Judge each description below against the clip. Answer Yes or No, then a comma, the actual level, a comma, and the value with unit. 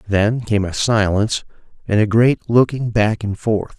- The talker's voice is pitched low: Yes, low, 110 Hz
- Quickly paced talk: No, average, 175 wpm